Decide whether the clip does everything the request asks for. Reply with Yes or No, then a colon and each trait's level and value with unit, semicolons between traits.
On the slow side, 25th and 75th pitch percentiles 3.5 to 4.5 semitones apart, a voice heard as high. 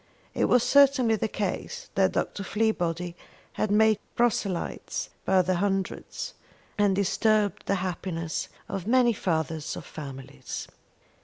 Yes: slow, 125 wpm; average, 3.8 semitones; high, 195 Hz